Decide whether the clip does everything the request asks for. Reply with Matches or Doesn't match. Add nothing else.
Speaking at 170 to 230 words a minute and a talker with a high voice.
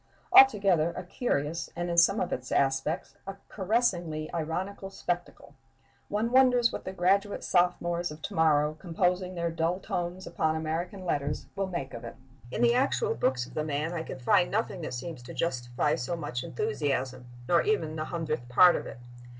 Doesn't match